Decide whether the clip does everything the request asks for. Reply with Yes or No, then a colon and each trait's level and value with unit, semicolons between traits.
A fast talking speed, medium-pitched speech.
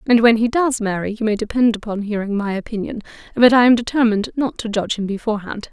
No: fast, 220 wpm; high, 220 Hz